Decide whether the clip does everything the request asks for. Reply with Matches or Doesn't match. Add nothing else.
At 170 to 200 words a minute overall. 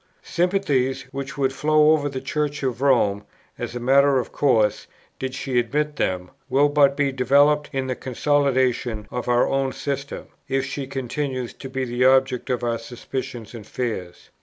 Matches